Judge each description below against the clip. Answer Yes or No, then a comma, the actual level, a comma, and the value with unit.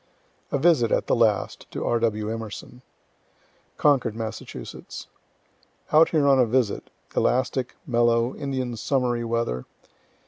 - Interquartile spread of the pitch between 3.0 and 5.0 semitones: No, narrow, 2.6 semitones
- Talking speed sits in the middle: No, slow, 125 wpm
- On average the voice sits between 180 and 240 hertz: No, low, 120 Hz